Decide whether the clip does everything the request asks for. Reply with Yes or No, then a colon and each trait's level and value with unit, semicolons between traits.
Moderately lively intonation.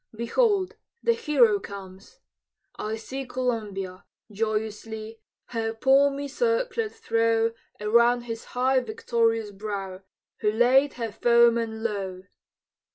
Yes: average, 3.7 semitones